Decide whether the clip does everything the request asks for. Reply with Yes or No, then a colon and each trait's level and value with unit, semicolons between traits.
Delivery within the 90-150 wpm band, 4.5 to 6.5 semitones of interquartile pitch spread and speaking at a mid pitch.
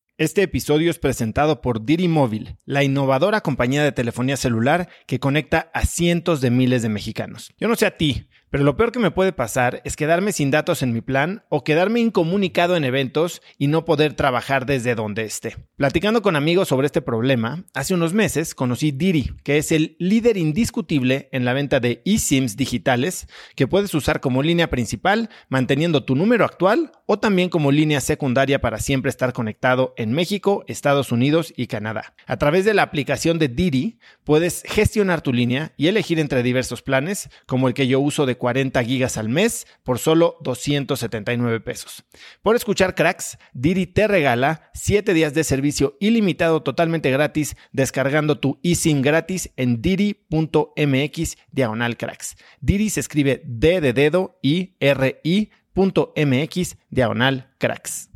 No: average, 165 wpm; average, 4.8 semitones; medium, 145 Hz